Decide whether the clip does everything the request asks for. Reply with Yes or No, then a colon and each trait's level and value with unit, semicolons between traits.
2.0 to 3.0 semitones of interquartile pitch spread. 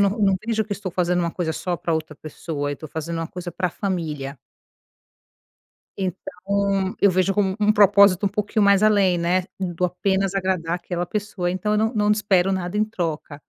Yes: narrow, 2.6 semitones